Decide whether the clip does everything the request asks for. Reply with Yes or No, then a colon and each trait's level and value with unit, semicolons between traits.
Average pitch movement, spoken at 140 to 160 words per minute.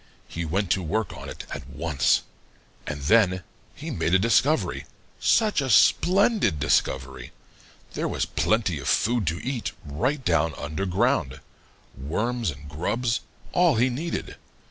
No: wide, 8.3 semitones; average, 145 wpm